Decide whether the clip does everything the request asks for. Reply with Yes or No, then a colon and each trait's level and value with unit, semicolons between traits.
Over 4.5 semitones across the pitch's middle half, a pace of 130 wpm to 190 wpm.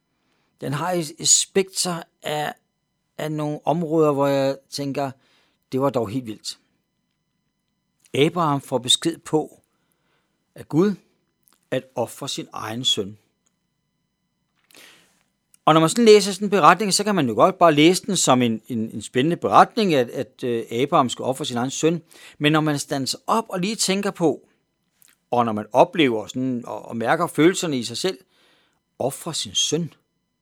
Yes: average, 4.9 semitones; average, 160 wpm